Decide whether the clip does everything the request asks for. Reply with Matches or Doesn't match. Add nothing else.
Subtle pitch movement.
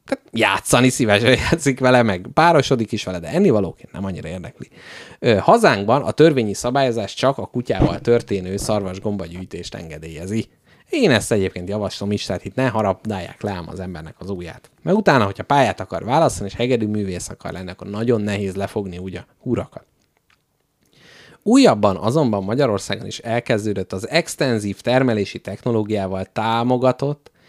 Doesn't match